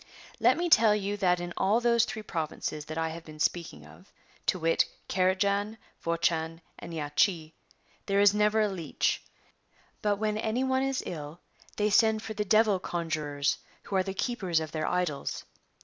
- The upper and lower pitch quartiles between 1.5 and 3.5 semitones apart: No, average, 4.6 semitones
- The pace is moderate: Yes, average, 180 wpm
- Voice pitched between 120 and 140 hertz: No, high, 190 Hz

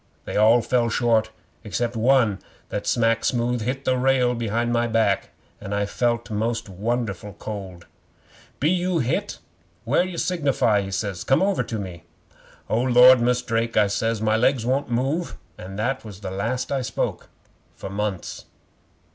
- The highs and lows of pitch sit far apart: No, average, 3.2 semitones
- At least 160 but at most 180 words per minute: Yes, average, 165 wpm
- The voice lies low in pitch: Yes, low, 115 Hz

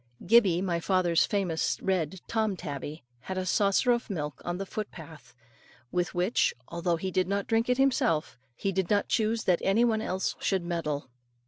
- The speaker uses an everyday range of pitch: Yes, average, 3.5 semitones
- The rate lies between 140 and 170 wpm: No, average, 185 wpm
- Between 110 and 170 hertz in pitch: No, medium, 185 Hz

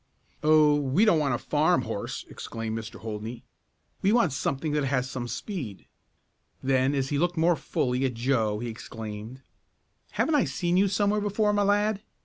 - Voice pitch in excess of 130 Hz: Yes, medium, 140 Hz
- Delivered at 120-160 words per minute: No, average, 170 wpm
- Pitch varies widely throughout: Yes, wide, 6.9 semitones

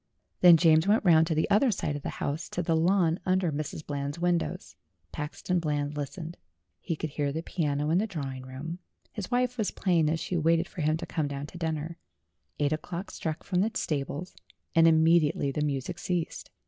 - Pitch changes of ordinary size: Yes, average, 3.1 semitones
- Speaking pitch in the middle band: Yes, medium, 160 Hz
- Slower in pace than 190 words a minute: No, average, 200 wpm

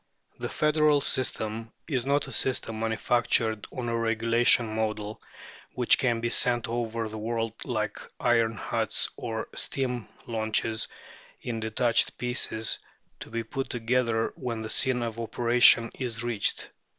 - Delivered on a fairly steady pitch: Yes, narrow, 1.7 semitones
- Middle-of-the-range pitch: No, low, 115 Hz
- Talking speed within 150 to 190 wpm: No, average, 140 wpm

